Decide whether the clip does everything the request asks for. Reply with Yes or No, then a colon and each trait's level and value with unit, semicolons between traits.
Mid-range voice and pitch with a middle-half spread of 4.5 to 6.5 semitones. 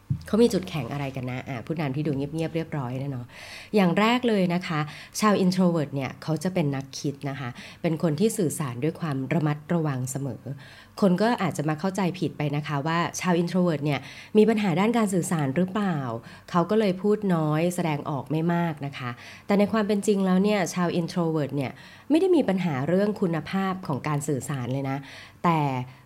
Yes: medium, 160 Hz; average, 5.1 semitones